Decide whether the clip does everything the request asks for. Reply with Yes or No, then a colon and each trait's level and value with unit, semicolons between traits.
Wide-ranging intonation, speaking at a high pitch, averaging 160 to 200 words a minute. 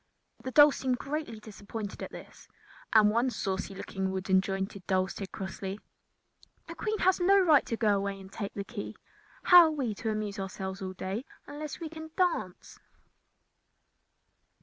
Yes: wide, 7.1 semitones; high, 215 Hz; average, 165 wpm